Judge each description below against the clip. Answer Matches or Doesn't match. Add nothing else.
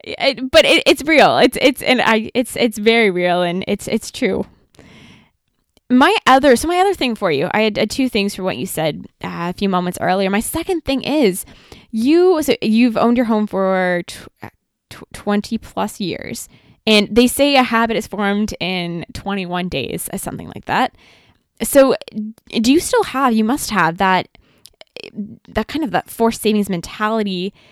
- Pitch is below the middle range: Doesn't match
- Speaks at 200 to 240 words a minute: Doesn't match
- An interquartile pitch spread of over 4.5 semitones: Matches